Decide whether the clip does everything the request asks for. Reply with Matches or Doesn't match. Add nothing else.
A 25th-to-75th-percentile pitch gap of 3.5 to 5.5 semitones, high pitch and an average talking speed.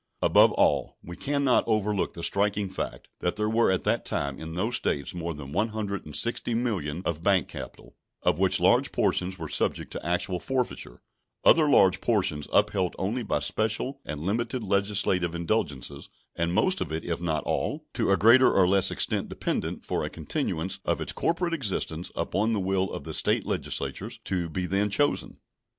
Doesn't match